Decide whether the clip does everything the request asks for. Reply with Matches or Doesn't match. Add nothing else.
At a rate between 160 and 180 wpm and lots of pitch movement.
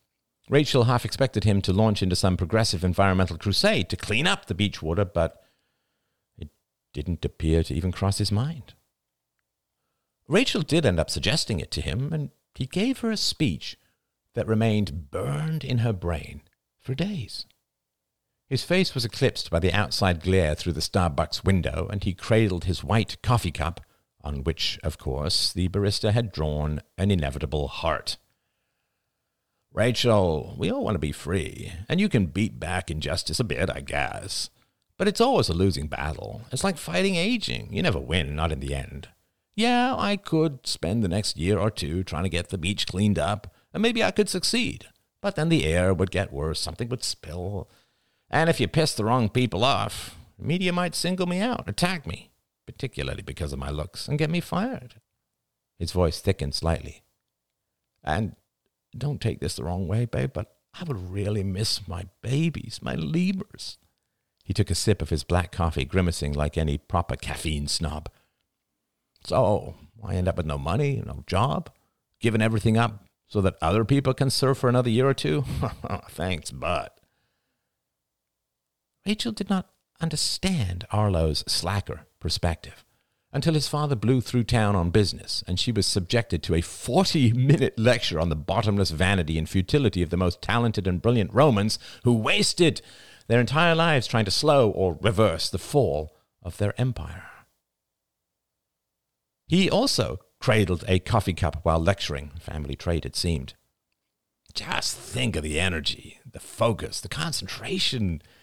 Matches